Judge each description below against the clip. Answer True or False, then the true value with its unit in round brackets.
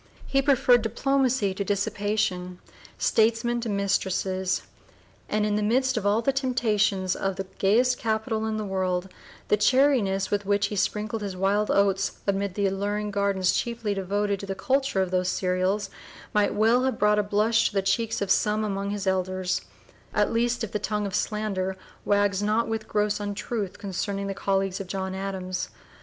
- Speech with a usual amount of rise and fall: False (2.3 semitones)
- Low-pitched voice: False (205 Hz)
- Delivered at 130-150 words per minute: False (175 wpm)